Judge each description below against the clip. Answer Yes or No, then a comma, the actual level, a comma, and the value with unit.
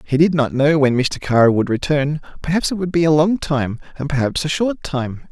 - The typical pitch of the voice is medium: Yes, medium, 145 Hz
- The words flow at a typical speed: No, fast, 235 wpm